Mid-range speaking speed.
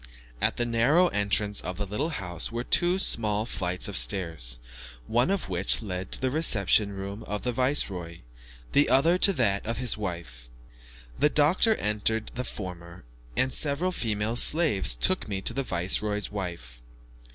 Yes: average, 165 wpm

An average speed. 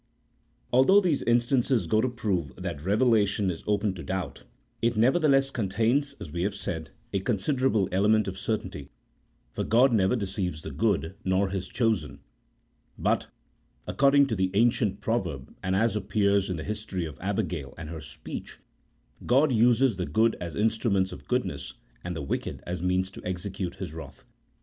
Yes: average, 165 wpm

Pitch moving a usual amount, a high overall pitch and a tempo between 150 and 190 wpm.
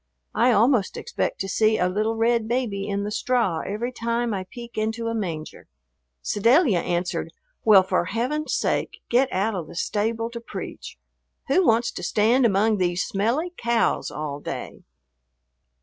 Yes: average, 3.3 semitones; high, 220 Hz; average, 160 wpm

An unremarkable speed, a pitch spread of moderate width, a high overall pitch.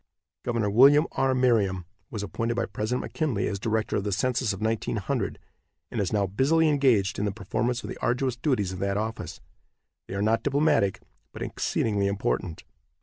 No: average, 175 wpm; average, 4.2 semitones; low, 110 Hz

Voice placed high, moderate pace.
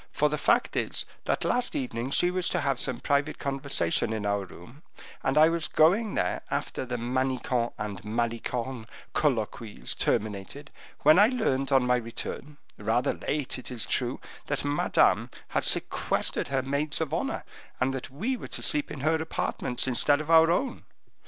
No: low, 135 Hz; average, 170 wpm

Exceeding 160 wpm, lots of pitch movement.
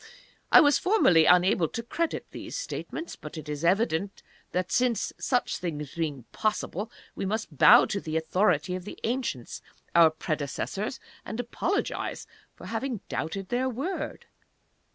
No: average, 140 wpm; wide, 7.1 semitones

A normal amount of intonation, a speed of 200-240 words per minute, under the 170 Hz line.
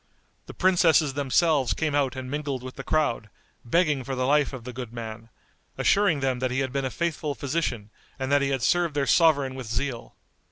Yes: average, 3.0 semitones; fast, 205 wpm; low, 135 Hz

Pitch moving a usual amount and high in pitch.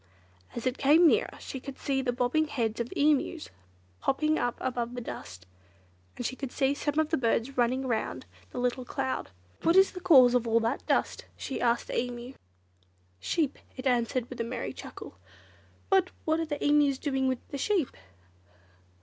Yes: average, 3.5 semitones; very high, 260 Hz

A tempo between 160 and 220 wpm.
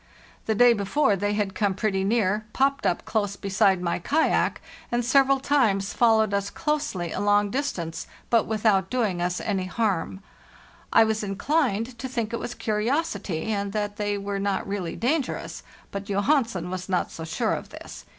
Yes: average, 175 wpm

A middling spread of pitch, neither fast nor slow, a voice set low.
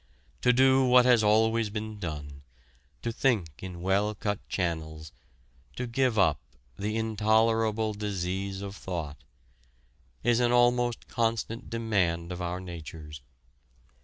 No: average, 4.6 semitones; slow, 125 wpm; low, 105 Hz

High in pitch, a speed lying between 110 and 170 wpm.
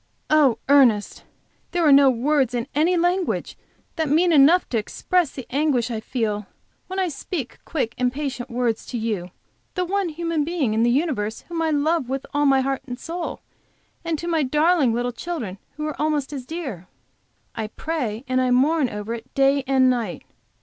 No: very high, 275 Hz; average, 180 wpm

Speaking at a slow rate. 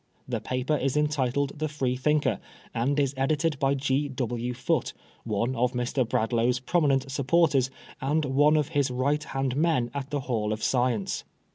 No: average, 165 wpm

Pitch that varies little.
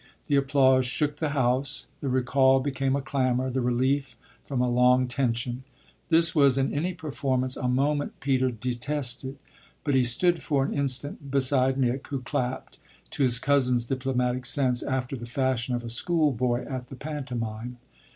Yes: narrow, 2.0 semitones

